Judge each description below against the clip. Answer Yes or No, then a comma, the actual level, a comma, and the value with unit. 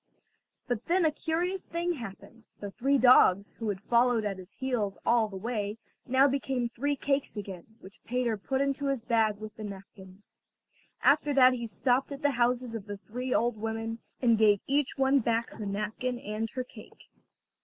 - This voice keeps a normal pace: Yes, average, 185 wpm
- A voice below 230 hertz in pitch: No, high, 235 Hz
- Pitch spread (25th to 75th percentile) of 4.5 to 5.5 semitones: No, average, 4.0 semitones